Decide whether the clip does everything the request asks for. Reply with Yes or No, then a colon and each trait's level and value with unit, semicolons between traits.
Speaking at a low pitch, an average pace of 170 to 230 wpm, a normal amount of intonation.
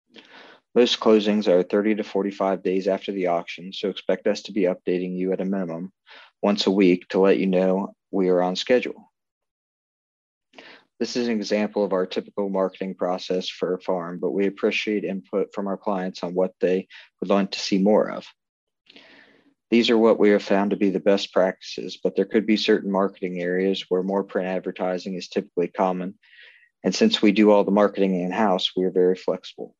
No: very low, 95 Hz; average, 195 wpm; narrow, 1.8 semitones